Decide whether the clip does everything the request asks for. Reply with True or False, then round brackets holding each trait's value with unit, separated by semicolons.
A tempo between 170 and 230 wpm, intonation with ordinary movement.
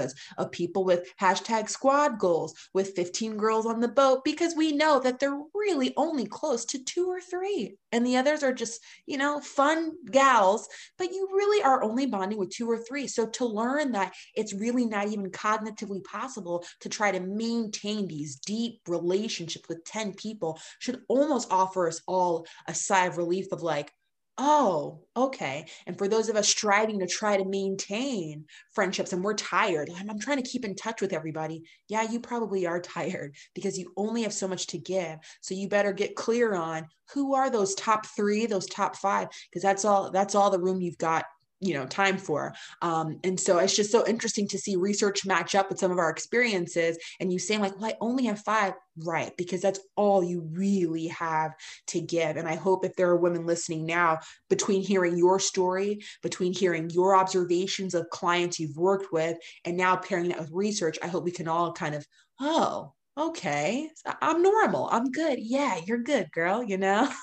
True (195 wpm; 4.6 semitones)